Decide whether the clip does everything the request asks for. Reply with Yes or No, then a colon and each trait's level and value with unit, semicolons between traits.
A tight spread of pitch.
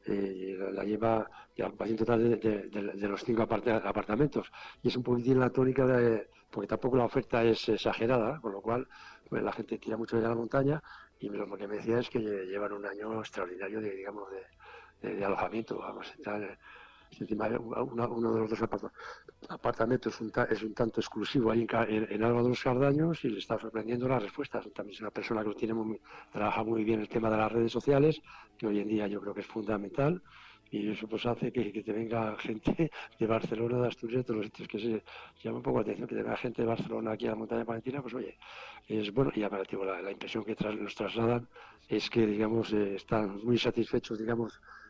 Yes: narrow, 2.0 semitones